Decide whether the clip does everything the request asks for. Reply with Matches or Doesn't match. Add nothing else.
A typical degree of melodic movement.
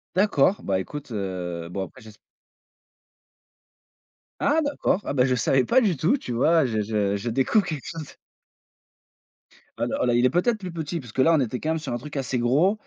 Doesn't match